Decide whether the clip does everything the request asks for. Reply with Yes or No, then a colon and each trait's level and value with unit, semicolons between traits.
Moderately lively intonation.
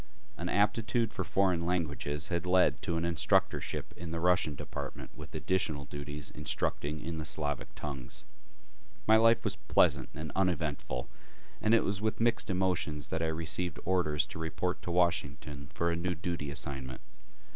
Yes: average, 3.8 semitones